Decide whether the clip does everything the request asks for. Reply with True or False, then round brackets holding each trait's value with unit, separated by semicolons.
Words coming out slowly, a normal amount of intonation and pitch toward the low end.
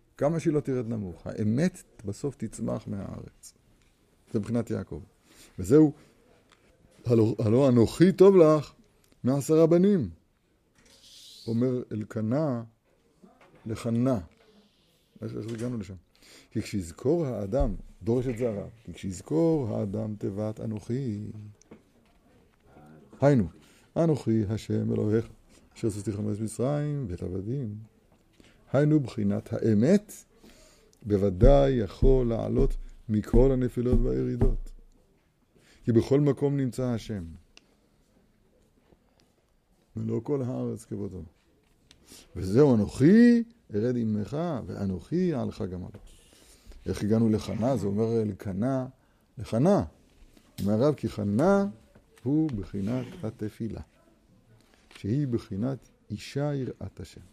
True (95 wpm; 4.2 semitones; 115 Hz)